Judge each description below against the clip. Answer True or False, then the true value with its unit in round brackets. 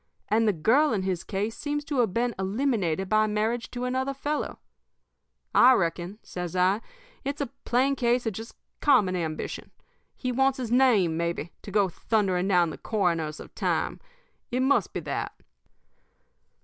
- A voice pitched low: False (215 Hz)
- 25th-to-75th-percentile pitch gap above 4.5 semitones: True (5.5 semitones)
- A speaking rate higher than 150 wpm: True (160 wpm)